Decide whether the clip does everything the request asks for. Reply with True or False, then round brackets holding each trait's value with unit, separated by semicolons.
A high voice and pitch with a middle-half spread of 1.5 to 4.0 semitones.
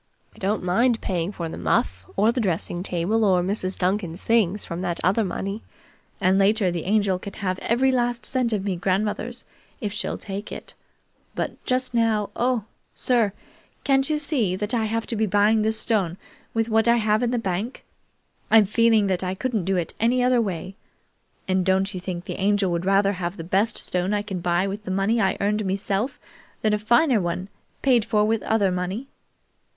True (205 Hz; 3.4 semitones)